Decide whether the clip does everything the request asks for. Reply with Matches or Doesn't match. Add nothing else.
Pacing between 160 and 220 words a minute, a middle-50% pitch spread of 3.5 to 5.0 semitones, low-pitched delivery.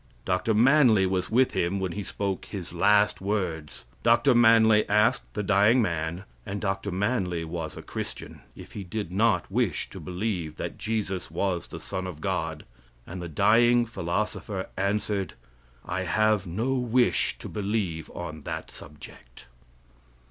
Doesn't match